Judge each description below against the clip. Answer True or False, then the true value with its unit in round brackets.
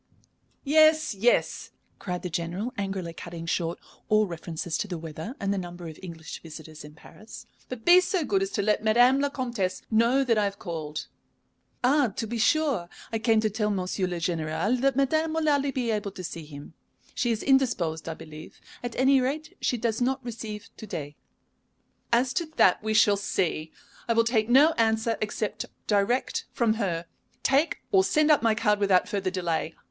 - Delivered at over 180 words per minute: True (190 wpm)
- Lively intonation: True (6.4 semitones)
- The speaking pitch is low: False (215 Hz)